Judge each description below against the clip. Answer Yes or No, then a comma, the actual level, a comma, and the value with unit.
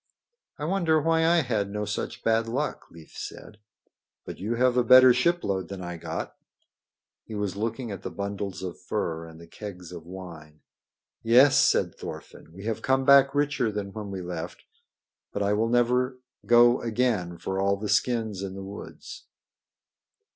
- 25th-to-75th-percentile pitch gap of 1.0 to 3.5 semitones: No, average, 4.7 semitones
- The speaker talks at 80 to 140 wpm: No, average, 170 wpm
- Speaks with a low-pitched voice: Yes, low, 105 Hz